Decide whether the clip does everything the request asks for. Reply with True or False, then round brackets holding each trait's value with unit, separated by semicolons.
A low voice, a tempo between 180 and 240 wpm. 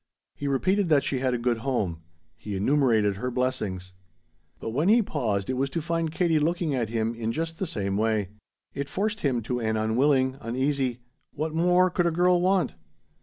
True (130 Hz; 190 wpm)